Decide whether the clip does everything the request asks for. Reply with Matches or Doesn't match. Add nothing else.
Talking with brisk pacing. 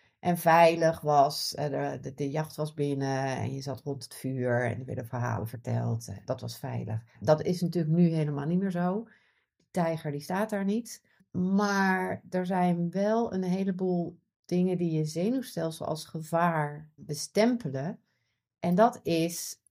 Doesn't match